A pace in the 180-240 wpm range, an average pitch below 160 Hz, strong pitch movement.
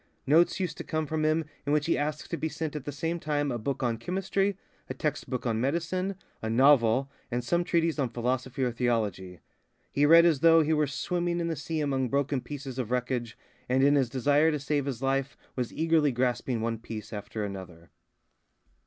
No: fast, 205 wpm; medium, 140 Hz; average, 4.5 semitones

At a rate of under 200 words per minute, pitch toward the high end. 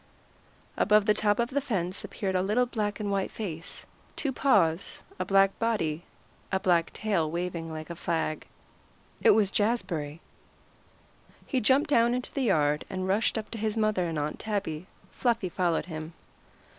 Yes: average, 170 wpm; high, 195 Hz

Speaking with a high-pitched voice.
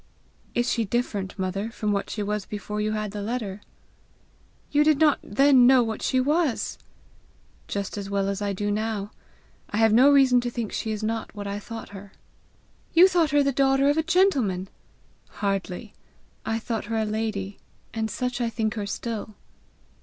Yes: high, 220 Hz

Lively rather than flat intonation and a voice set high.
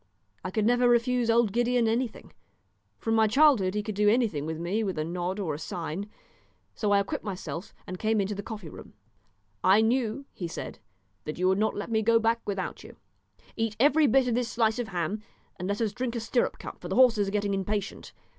No: average, 3.3 semitones; high, 215 Hz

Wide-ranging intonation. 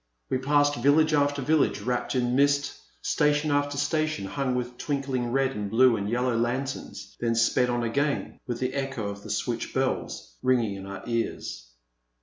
No: average, 3.4 semitones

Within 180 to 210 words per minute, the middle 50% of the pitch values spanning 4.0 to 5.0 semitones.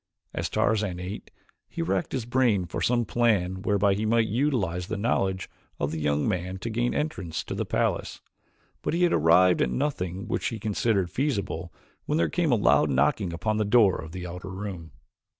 Yes: average, 190 wpm; average, 4.6 semitones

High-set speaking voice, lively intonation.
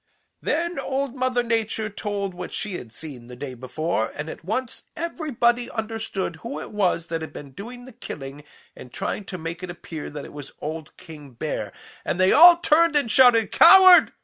Yes: high, 200 Hz; wide, 7.9 semitones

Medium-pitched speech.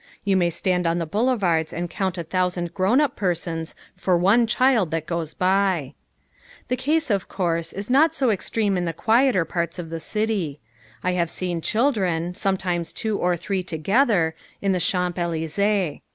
Yes: medium, 180 Hz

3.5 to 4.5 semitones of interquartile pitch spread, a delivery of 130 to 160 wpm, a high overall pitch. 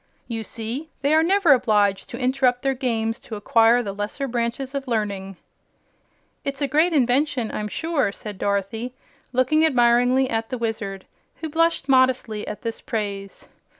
Yes: average, 3.9 semitones; average, 155 wpm; high, 245 Hz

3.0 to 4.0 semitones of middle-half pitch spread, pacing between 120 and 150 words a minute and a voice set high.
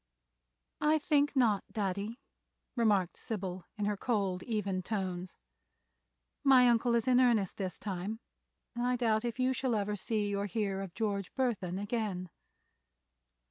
Yes: average, 3.7 semitones; average, 140 wpm; high, 210 Hz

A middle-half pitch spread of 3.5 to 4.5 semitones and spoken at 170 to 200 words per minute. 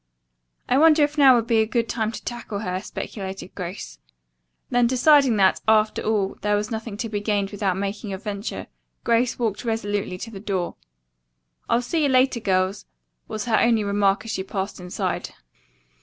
No: average, 3.0 semitones; average, 180 wpm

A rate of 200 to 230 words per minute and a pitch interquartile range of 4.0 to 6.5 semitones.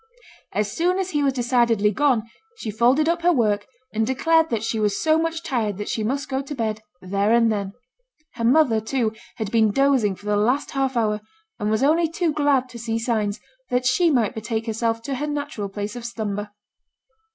Yes: fast, 205 wpm; average, 4.7 semitones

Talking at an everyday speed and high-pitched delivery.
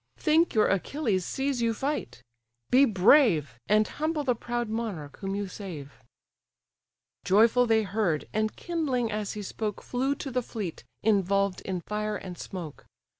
Yes: average, 150 wpm; high, 215 Hz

